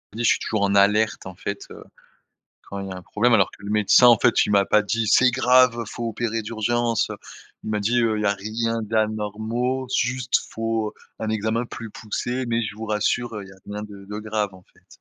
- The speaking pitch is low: Yes, low, 110 Hz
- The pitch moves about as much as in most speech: No, narrow, 2.0 semitones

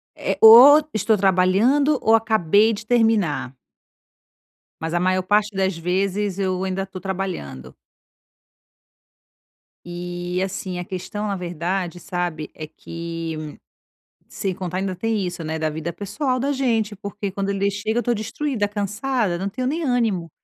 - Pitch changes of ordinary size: Yes, average, 3.7 semitones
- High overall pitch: Yes, high, 195 Hz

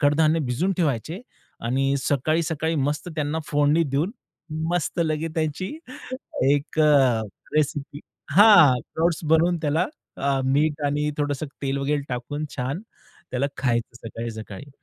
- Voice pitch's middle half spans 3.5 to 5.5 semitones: No, average, 2.7 semitones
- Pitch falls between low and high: Yes, medium, 145 Hz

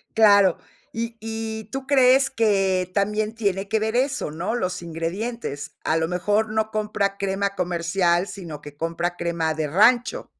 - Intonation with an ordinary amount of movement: Yes, average, 4.3 semitones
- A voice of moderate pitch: No, high, 200 Hz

